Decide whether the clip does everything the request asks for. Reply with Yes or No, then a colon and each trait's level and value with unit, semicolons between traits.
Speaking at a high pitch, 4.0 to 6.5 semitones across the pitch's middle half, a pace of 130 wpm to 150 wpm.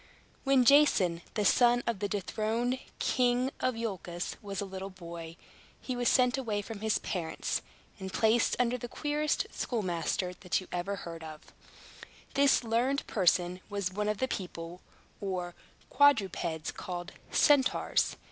Yes: high, 205 Hz; average, 5.2 semitones; average, 145 wpm